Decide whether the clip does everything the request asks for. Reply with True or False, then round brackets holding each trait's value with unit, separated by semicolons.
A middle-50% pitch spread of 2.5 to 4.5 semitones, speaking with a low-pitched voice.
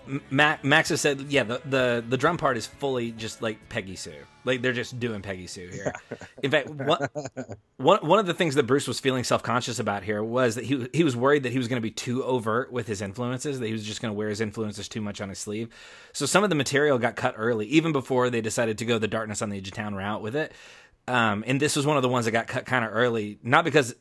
True (3.9 semitones; 125 Hz)